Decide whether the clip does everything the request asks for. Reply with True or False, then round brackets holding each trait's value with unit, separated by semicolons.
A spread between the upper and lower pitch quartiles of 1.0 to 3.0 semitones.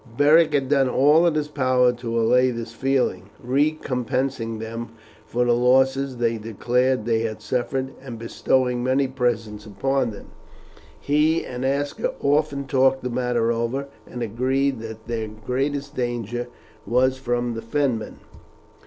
True (2.7 semitones)